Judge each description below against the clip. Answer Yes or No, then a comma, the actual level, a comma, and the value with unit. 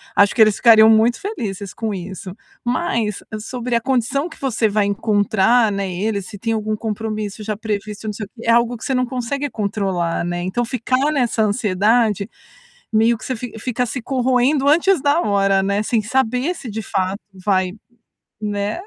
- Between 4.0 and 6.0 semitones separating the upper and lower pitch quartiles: No, average, 3.5 semitones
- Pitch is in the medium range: No, high, 220 Hz